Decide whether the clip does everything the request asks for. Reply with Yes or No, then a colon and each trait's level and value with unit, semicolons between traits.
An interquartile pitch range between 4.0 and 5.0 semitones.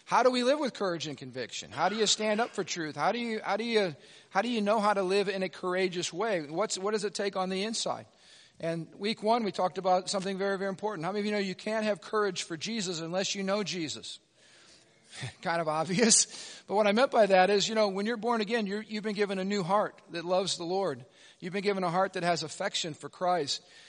No: average, 2.8 semitones